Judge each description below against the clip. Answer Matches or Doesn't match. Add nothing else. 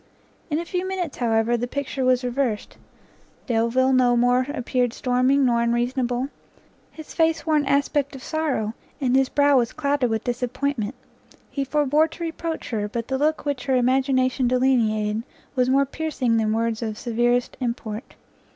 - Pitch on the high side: Matches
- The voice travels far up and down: Doesn't match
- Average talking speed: Matches